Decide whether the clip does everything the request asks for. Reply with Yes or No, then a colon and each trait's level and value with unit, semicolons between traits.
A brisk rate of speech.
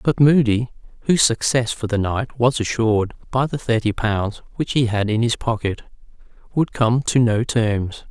No: average, 180 wpm